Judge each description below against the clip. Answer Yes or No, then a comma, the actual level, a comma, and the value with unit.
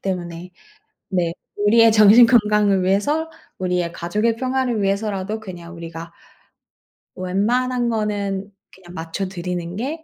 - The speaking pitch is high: Yes, high, 200 Hz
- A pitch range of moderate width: Yes, average, 4.0 semitones